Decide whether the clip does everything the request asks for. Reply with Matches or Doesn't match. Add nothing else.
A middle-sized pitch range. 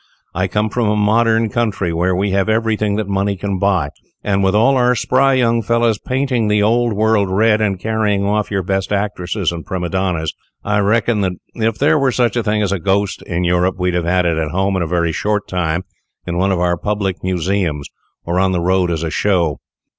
Matches